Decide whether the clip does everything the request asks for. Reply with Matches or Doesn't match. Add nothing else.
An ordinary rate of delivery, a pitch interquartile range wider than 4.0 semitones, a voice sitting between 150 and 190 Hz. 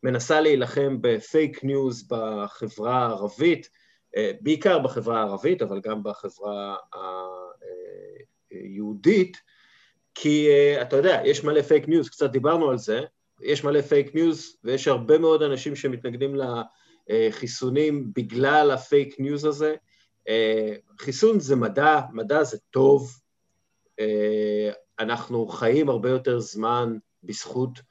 Doesn't match